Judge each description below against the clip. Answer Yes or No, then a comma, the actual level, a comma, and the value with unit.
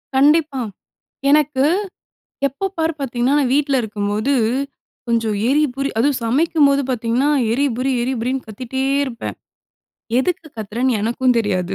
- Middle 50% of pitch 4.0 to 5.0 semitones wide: No, average, 3.5 semitones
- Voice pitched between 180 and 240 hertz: No, very high, 260 Hz